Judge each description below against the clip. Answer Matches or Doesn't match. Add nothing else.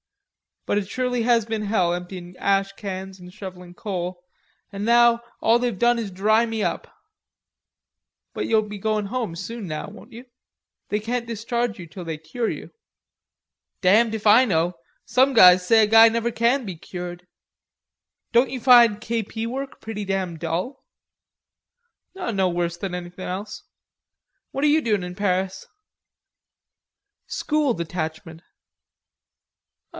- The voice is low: Doesn't match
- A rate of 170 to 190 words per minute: Doesn't match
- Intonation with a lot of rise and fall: Doesn't match